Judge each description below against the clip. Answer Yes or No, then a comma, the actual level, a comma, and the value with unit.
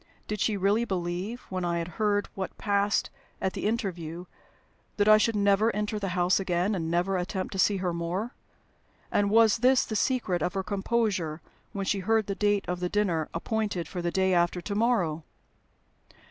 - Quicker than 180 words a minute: Yes, average, 190 wpm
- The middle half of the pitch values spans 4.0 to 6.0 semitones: No, average, 3.0 semitones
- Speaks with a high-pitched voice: Yes, high, 195 Hz